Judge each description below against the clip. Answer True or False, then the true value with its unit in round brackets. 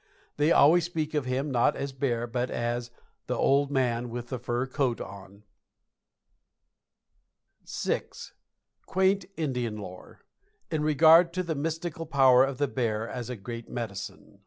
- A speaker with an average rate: True (150 wpm)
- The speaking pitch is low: True (130 Hz)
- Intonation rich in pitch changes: False (4.3 semitones)